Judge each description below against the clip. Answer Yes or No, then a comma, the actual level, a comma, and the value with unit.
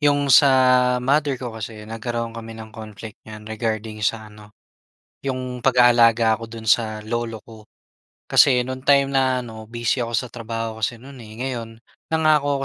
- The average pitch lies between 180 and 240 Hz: No, low, 115 Hz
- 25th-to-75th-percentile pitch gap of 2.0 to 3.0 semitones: Yes, narrow, 2.6 semitones